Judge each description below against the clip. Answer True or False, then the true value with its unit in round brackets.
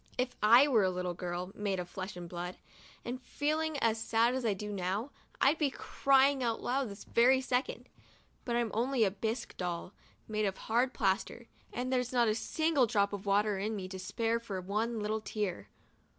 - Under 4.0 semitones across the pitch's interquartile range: False (4.3 semitones)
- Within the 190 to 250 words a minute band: True (195 wpm)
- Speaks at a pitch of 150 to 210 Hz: False (220 Hz)